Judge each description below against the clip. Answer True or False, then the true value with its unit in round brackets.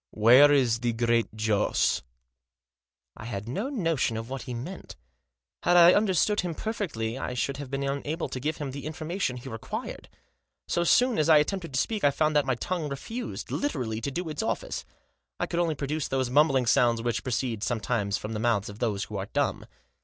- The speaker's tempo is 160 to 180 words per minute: False (205 wpm)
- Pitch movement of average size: False (5.7 semitones)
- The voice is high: False (135 Hz)